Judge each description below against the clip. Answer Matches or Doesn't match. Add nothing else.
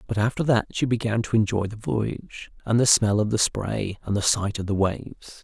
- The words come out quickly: Matches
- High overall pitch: Doesn't match